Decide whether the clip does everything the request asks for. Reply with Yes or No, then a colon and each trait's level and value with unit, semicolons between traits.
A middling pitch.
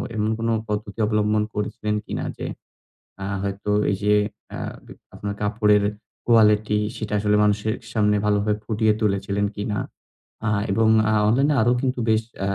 No: low, 105 Hz